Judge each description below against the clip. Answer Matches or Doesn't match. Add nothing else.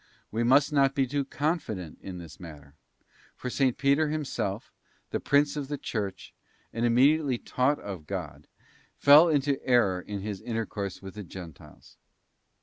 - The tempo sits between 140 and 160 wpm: Matches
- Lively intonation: Matches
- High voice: Doesn't match